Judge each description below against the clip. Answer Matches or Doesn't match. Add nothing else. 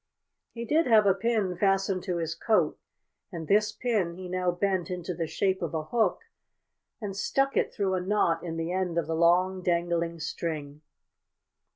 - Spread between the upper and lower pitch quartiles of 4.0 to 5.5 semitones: Doesn't match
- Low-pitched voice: Doesn't match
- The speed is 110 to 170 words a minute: Doesn't match